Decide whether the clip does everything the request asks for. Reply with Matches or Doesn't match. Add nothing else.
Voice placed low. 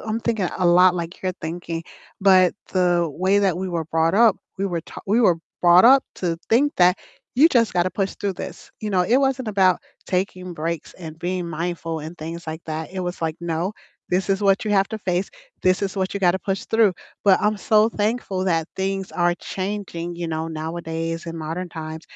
Doesn't match